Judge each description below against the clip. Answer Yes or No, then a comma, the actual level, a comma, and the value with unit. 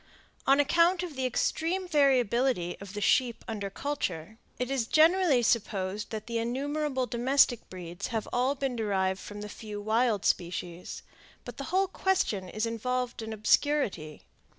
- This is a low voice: No, high, 240 Hz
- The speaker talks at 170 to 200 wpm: No, average, 150 wpm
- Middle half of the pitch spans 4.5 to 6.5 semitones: Yes, average, 5.1 semitones